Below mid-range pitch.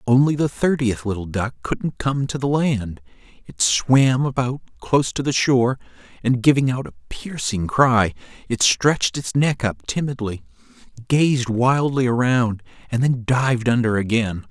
Yes: low, 125 Hz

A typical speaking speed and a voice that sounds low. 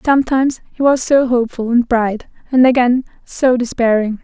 No: average, 155 wpm; high, 245 Hz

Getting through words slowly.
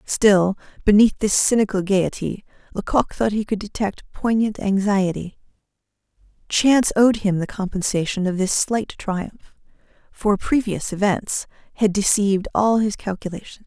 Yes: slow, 125 wpm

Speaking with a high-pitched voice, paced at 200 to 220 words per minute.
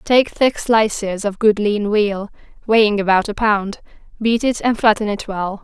No: high, 210 Hz; average, 180 wpm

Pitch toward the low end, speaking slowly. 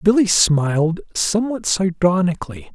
No: medium, 180 Hz; slow, 85 wpm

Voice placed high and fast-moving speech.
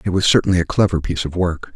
No: very low, 90 Hz; fast, 275 wpm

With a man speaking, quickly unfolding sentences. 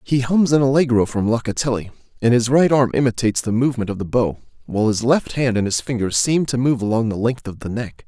Yes: male; fast, 240 wpm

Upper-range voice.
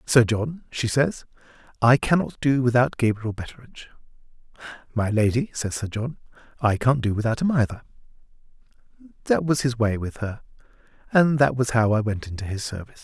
No: low, 120 Hz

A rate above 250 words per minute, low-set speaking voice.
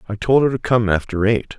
Yes: fast, 265 wpm; low, 110 Hz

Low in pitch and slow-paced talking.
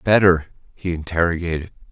Yes: very low, 85 Hz; slow, 95 wpm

